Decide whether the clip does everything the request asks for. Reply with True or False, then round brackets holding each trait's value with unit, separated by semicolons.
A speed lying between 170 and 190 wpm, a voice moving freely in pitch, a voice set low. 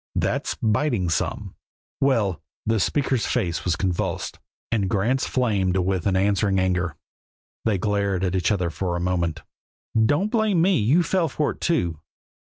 False (155 wpm; 6.2 semitones; 100 Hz)